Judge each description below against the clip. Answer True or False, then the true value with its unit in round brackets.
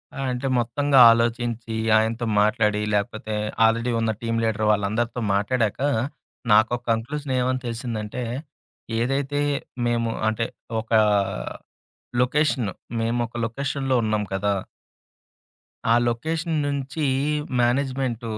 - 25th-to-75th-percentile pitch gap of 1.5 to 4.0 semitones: True (2.8 semitones)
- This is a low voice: True (120 Hz)